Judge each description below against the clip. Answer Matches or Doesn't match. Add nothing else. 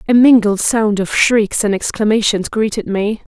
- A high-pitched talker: Matches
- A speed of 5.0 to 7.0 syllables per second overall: Doesn't match